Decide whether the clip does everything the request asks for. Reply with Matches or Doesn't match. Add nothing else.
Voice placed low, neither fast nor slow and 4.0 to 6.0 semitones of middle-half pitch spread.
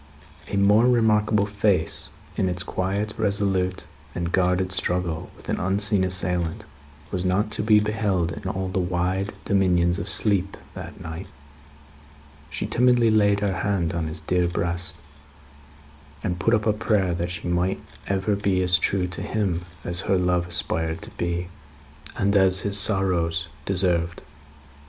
Doesn't match